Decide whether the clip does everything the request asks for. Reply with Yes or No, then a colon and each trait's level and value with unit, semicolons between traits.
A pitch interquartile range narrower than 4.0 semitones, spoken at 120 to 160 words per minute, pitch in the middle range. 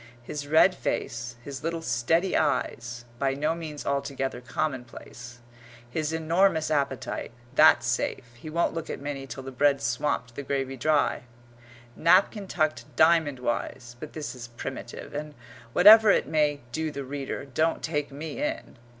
Yes: average, 3.6 semitones; average, 150 wpm; medium, 145 Hz